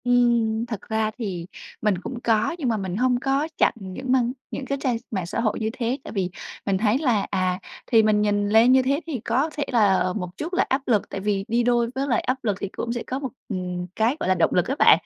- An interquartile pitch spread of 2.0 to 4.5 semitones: Yes, average, 4.1 semitones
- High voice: Yes, high, 230 Hz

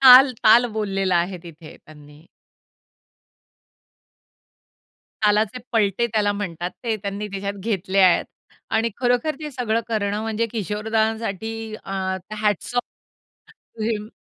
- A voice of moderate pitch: No, high, 215 Hz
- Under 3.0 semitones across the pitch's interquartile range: Yes, narrow, 2.5 semitones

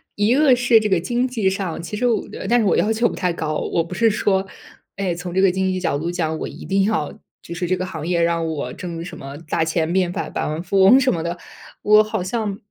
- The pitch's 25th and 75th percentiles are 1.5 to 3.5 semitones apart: No, average, 4.1 semitones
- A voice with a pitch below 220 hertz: Yes, medium, 185 Hz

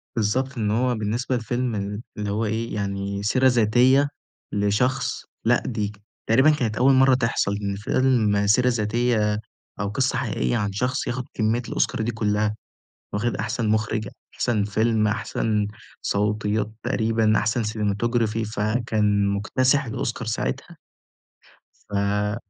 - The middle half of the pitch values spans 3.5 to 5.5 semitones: No, average, 2.8 semitones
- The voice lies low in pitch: Yes, low, 110 Hz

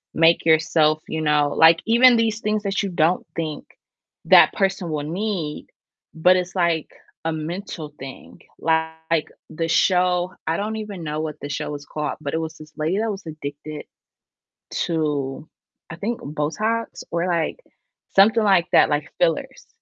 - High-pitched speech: No, medium, 165 Hz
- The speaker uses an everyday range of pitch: Yes, average, 3.9 semitones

